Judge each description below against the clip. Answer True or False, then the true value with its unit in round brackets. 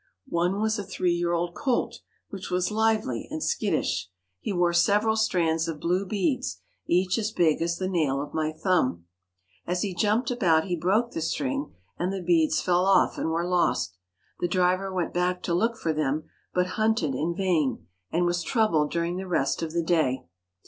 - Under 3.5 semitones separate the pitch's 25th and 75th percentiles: True (3.1 semitones)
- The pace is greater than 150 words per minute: True (190 wpm)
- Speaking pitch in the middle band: True (175 Hz)